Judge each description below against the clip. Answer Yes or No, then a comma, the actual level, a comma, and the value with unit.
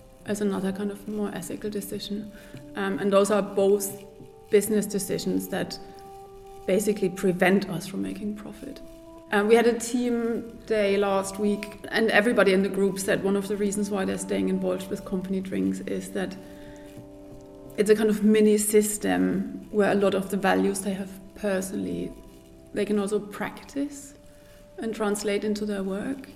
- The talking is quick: No, average, 165 wpm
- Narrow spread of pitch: Yes, narrow, 1.9 semitones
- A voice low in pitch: No, high, 200 Hz